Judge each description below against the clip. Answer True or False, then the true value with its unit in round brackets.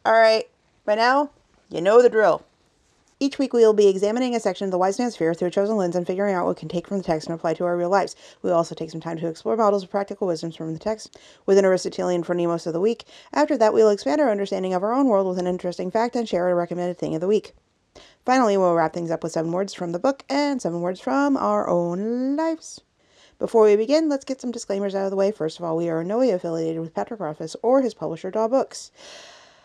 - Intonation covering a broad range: True (5.7 semitones)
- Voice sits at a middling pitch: False (200 Hz)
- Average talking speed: False (270 wpm)